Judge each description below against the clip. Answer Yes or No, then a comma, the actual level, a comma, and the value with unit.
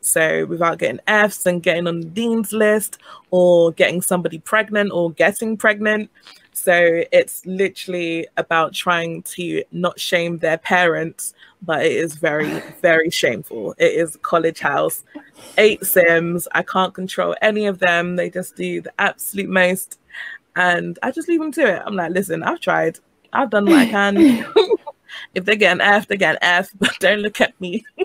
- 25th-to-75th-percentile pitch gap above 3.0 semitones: Yes, average, 4.0 semitones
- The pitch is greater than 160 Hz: Yes, medium, 185 Hz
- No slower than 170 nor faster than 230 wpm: Yes, average, 175 wpm